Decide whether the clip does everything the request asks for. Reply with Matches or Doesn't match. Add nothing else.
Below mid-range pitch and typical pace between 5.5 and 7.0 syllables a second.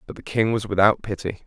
Matches